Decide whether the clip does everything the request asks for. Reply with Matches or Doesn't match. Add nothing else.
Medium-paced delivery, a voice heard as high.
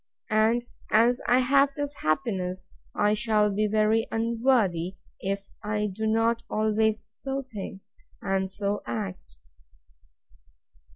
Doesn't match